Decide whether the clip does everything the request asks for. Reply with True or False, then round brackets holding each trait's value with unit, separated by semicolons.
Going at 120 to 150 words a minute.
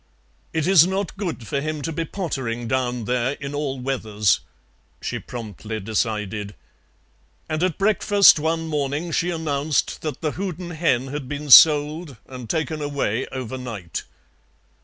True (140 wpm)